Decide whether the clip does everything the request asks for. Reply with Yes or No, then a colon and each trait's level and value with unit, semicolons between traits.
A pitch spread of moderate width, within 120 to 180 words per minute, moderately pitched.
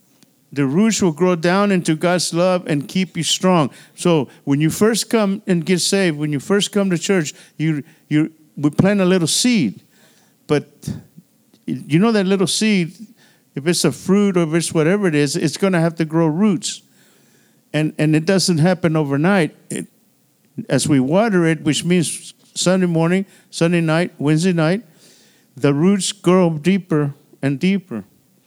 Yes: average, 3.7 semitones; average, 170 wpm; medium, 175 Hz